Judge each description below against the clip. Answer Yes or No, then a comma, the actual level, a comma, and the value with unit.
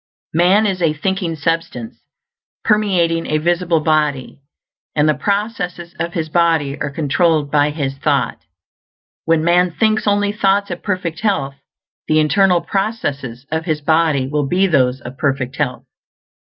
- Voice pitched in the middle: Yes, medium, 165 Hz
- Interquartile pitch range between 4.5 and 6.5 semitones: No, average, 4.0 semitones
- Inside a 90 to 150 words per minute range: Yes, average, 145 wpm